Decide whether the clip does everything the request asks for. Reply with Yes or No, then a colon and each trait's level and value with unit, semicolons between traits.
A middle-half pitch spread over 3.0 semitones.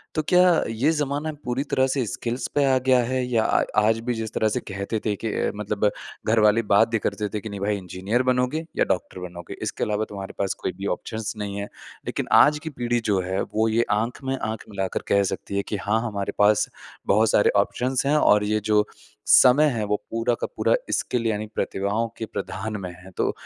Yes: average, 3.5 semitones